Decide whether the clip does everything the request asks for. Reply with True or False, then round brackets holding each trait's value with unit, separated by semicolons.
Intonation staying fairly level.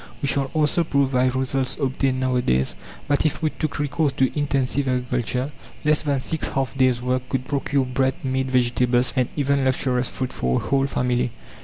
True (1.8 semitones)